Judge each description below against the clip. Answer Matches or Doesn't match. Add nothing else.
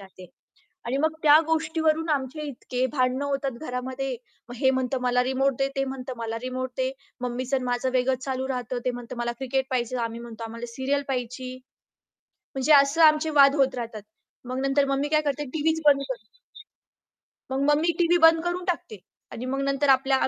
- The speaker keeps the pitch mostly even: Matches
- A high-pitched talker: Matches